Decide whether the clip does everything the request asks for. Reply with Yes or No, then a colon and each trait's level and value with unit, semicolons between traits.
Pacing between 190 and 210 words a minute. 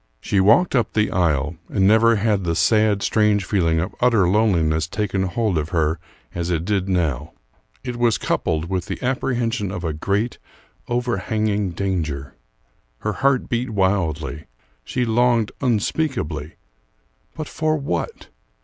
No: average, 140 wpm